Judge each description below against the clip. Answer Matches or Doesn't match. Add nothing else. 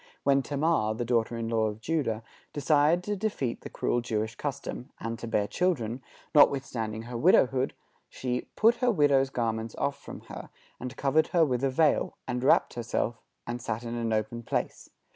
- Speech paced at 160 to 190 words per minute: Matches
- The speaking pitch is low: Matches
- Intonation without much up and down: Doesn't match